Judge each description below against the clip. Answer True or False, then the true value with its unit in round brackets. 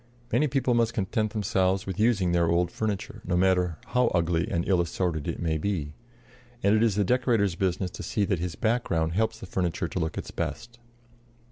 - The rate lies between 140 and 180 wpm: False (200 wpm)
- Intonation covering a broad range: False (4.1 semitones)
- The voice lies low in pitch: True (95 Hz)